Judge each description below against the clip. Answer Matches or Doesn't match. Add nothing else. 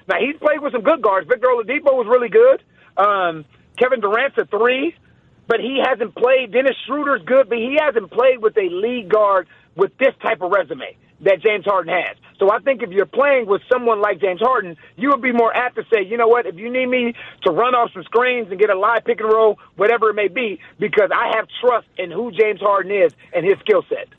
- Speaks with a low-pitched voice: Doesn't match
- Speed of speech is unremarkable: Doesn't match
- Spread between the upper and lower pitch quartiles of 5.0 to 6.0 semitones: Matches